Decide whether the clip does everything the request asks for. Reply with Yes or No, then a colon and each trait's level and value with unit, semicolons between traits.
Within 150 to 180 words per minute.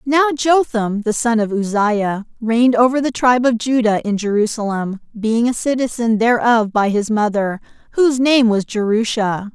Yes: average, 155 wpm